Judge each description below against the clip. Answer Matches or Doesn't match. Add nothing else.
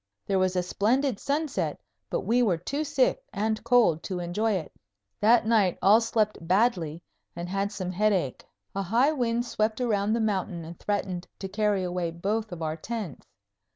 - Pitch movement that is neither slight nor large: Matches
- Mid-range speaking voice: Doesn't match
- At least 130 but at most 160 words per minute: Doesn't match